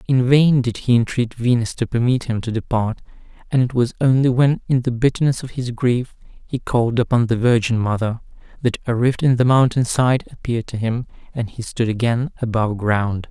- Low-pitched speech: Yes, low, 120 Hz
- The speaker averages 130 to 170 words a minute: No, average, 200 wpm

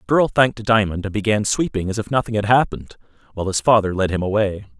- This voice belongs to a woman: No, male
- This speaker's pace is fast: Yes, fast, 225 wpm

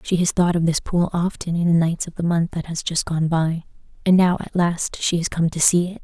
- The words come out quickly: Yes, fast, 280 wpm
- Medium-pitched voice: Yes, medium, 170 Hz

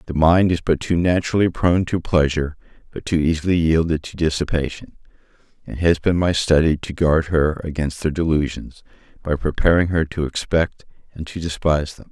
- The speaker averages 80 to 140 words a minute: No, average, 175 wpm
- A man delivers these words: Yes, male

